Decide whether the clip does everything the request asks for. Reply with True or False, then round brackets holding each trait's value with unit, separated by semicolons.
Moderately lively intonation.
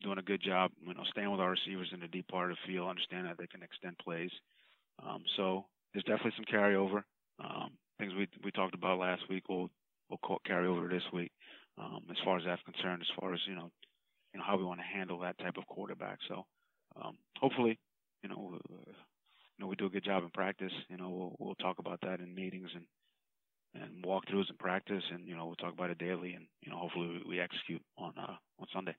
False (1.5 semitones)